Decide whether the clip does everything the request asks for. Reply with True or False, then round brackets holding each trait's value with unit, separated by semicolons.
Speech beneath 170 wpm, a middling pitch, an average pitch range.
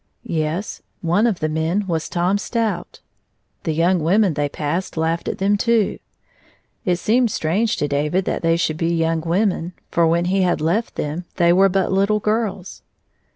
False (175 wpm; 175 Hz; 3.5 semitones)